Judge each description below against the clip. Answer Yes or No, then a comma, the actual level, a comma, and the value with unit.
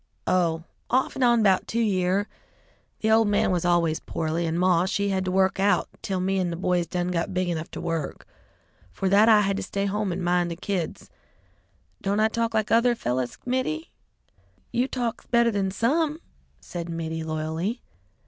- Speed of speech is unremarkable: Yes, average, 185 wpm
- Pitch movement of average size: Yes, average, 4.1 semitones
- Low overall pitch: No, high, 190 Hz